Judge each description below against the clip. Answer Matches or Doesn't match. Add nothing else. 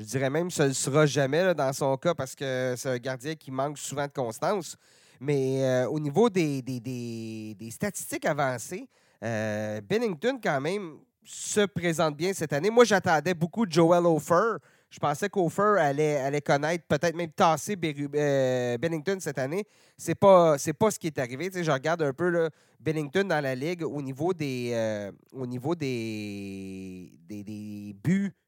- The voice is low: Doesn't match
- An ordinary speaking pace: Matches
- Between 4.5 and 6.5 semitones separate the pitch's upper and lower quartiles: Matches